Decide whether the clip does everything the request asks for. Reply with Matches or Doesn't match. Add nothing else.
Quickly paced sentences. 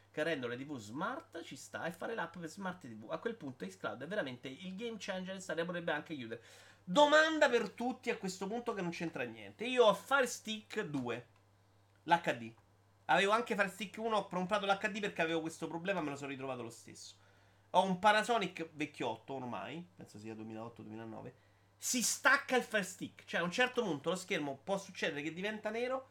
Matches